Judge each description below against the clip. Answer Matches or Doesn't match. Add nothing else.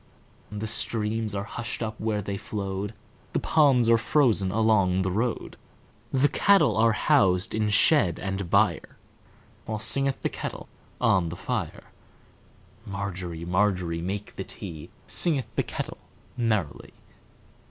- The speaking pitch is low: Matches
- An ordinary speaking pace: Doesn't match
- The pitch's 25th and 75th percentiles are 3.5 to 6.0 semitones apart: Doesn't match